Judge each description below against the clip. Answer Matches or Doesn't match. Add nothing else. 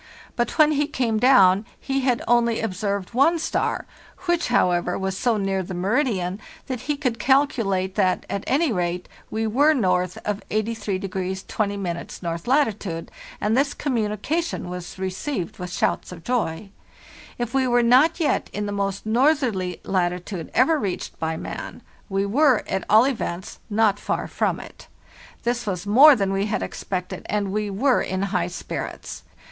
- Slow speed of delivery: Doesn't match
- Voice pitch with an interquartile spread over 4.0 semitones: Matches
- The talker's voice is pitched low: Doesn't match